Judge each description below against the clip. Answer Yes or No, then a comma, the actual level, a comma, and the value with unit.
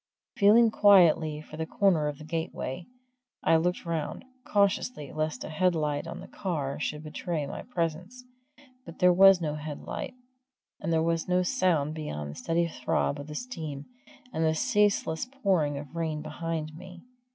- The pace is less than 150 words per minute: No, average, 165 wpm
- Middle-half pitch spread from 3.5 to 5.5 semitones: No, average, 3.1 semitones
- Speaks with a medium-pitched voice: Yes, medium, 160 Hz